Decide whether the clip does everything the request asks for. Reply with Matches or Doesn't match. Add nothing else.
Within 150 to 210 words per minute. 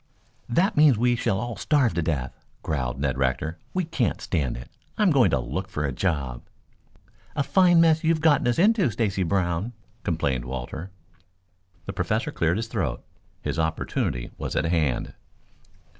Matches